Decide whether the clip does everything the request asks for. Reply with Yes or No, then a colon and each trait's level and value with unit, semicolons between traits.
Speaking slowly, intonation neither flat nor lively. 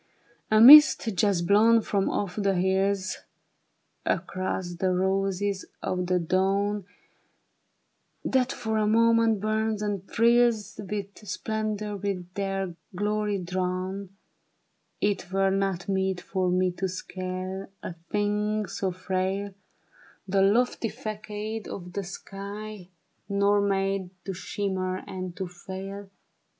No: slow, 125 wpm; narrow, 1.9 semitones